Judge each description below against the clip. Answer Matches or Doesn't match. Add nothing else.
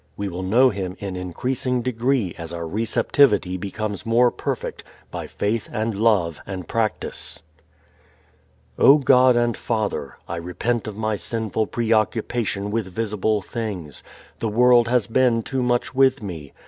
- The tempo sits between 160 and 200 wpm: Doesn't match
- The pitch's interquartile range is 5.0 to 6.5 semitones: Doesn't match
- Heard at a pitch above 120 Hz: Doesn't match